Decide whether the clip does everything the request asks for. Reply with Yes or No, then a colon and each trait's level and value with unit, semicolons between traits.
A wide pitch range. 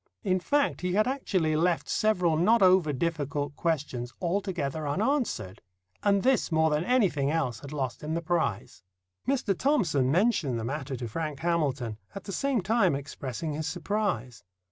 Yes: wide, 5.8 semitones